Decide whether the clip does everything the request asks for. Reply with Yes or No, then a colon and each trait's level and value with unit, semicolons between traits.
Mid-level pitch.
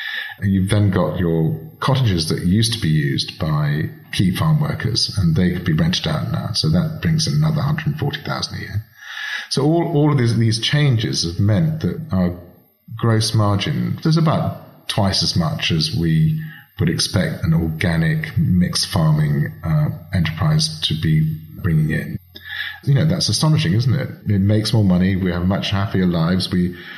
No: low, 110 Hz